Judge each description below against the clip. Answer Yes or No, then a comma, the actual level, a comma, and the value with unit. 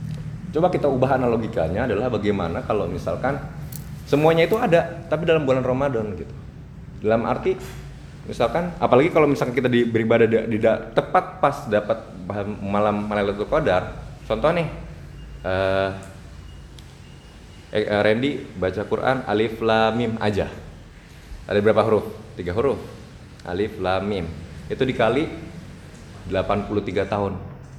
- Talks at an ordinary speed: Yes, average, 115 wpm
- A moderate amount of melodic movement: No, wide, 5.7 semitones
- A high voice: No, low, 110 Hz